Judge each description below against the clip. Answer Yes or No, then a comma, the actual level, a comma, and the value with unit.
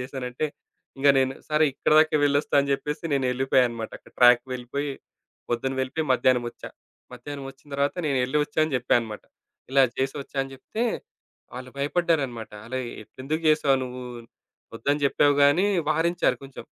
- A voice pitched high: No, low, 135 Hz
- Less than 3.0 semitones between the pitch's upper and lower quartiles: Yes, narrow, 2.6 semitones